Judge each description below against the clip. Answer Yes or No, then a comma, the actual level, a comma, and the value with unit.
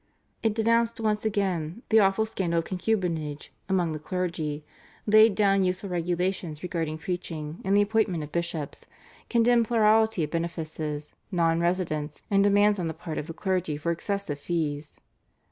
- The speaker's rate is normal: Yes, average, 150 wpm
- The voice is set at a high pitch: No, medium, 180 Hz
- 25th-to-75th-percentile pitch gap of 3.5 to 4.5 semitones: Yes, average, 4.2 semitones